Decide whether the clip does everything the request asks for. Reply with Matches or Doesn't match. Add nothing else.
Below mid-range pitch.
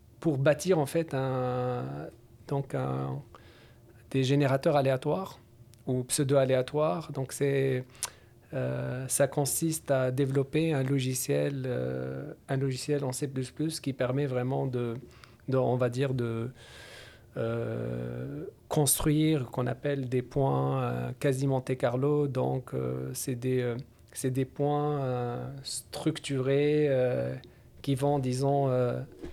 Matches